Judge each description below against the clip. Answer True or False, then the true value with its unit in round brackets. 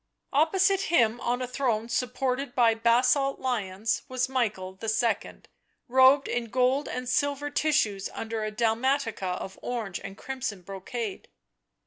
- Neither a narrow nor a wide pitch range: True (3.3 semitones)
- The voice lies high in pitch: True (245 Hz)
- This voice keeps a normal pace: False (130 wpm)